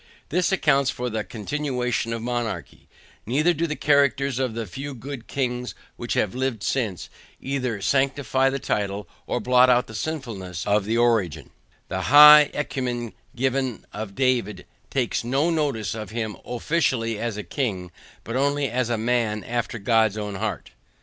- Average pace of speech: Yes, average, 160 wpm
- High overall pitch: No, low, 125 Hz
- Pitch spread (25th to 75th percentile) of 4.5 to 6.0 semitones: No, average, 3.8 semitones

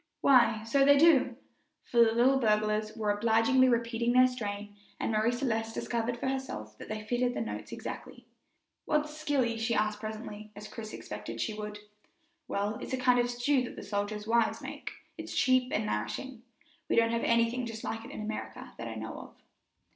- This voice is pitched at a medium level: No, high, 230 Hz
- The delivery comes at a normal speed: Yes, average, 190 wpm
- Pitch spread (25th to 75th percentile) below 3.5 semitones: Yes, average, 2.8 semitones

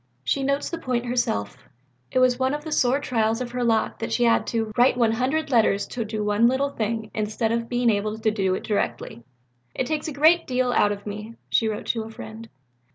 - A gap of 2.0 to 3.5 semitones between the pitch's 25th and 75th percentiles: Yes, average, 2.8 semitones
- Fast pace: Yes, fast, 225 wpm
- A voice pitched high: Yes, high, 230 Hz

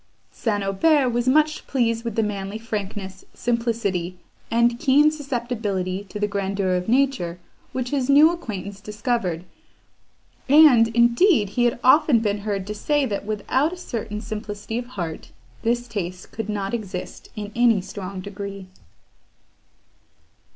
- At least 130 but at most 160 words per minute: Yes, average, 140 wpm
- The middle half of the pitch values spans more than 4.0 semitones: No, average, 3.6 semitones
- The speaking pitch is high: Yes, high, 220 Hz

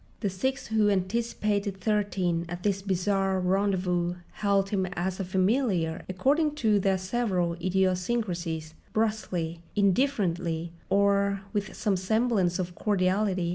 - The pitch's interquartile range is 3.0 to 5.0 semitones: No, narrow, 2.6 semitones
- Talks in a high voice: Yes, high, 195 Hz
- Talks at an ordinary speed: No, slow, 125 wpm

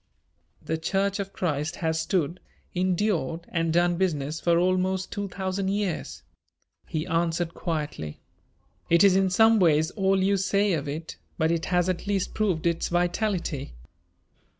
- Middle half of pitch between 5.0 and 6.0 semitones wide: No, average, 2.9 semitones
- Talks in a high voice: No, medium, 175 Hz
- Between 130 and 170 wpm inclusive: Yes, average, 150 wpm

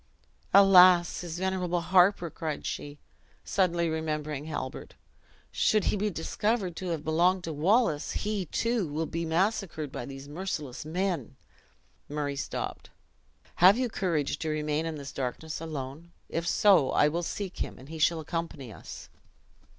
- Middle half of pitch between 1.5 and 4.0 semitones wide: Yes, average, 3.6 semitones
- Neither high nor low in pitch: Yes, medium, 165 Hz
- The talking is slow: No, average, 150 wpm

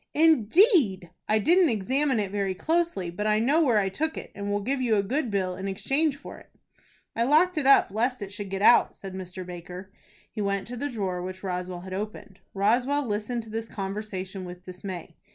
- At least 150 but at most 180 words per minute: No, fast, 205 wpm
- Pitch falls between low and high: No, high, 210 Hz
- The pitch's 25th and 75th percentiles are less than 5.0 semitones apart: No, wide, 5.5 semitones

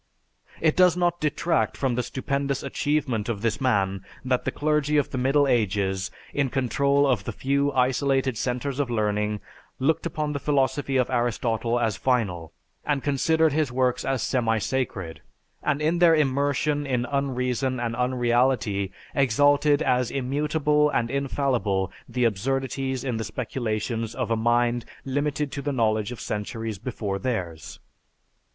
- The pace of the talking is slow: No, average, 150 wpm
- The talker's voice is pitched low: Yes, low, 130 Hz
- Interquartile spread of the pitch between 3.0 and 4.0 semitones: Yes, average, 3.6 semitones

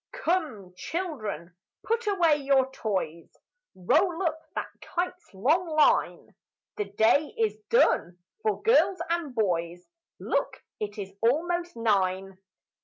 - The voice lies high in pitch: Yes, very high, 275 Hz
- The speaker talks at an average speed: No, slow, 115 wpm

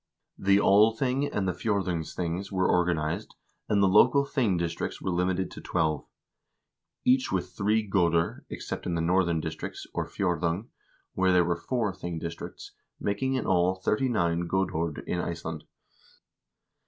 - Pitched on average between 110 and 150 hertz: No, very low, 95 Hz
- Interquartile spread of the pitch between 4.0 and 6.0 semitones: No, average, 3.4 semitones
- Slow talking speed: No, average, 145 wpm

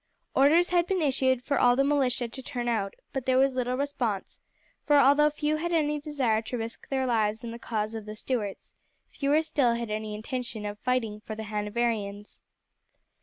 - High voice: Yes, high, 245 Hz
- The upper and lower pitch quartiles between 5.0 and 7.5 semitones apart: No, average, 4.4 semitones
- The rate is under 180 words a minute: No, average, 190 wpm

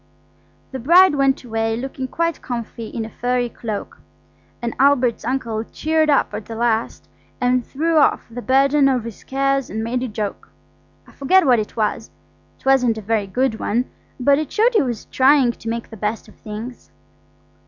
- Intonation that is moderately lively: Yes, average, 3.4 semitones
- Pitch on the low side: No, high, 245 Hz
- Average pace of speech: Yes, average, 185 wpm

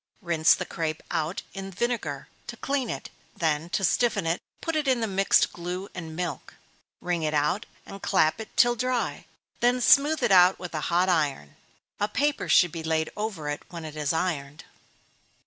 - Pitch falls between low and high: Yes, medium, 180 Hz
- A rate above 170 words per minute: Yes, average, 185 wpm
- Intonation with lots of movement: Yes, wide, 5.7 semitones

